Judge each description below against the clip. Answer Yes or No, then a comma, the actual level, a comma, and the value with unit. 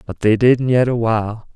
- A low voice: Yes, low, 115 Hz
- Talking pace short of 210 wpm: No, fast, 230 wpm